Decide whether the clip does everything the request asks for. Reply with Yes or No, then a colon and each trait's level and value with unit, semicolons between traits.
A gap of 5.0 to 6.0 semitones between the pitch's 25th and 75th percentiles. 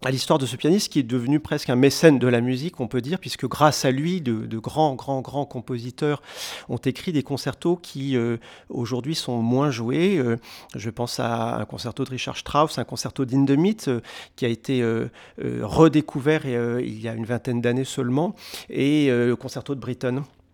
No: average, 3.2 semitones